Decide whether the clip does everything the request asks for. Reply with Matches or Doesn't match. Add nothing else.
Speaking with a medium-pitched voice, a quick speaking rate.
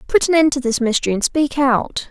Doesn't match